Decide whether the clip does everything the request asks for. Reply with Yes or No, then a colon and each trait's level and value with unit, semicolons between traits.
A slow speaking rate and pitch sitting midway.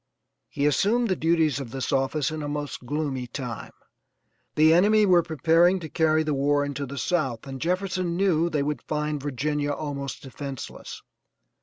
No: average, 165 wpm; medium, 150 Hz